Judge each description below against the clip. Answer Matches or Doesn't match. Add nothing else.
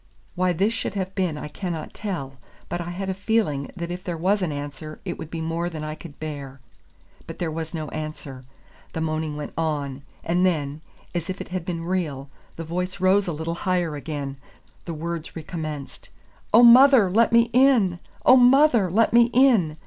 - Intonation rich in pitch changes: Doesn't match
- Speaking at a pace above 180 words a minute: Matches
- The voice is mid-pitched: Matches